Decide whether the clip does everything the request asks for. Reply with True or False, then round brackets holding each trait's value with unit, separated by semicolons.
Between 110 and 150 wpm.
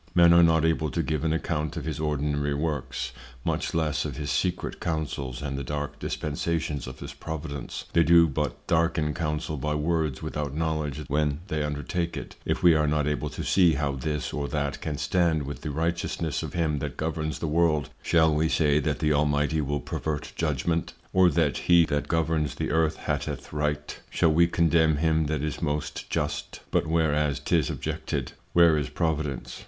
False (190 wpm)